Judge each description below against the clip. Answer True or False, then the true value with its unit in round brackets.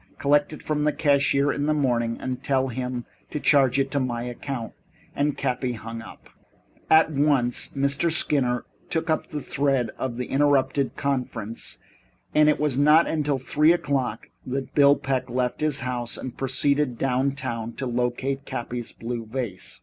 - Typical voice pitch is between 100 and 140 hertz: True (135 Hz)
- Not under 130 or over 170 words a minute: True (165 wpm)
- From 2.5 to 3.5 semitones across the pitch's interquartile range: True (2.8 semitones)